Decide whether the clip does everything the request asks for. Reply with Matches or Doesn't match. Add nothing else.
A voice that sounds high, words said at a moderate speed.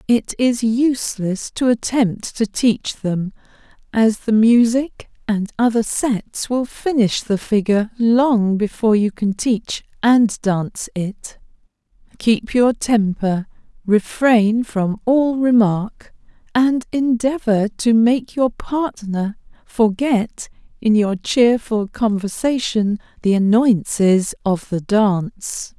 Doesn't match